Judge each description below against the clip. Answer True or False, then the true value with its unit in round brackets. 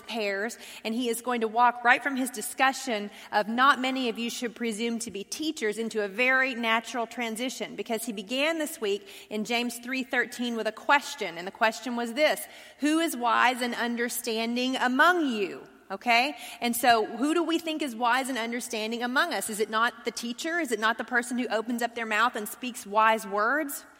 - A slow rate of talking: False (205 wpm)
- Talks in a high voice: True (235 Hz)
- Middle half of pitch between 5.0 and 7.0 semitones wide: False (2.6 semitones)